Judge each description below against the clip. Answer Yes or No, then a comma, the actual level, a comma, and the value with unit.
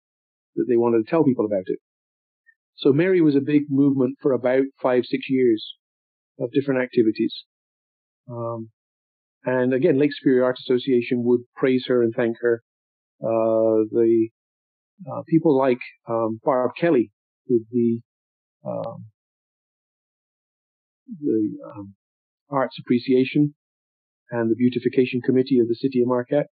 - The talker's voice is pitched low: Yes, low, 125 Hz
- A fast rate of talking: No, slow, 135 wpm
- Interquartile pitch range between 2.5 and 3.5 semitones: Yes, average, 3.2 semitones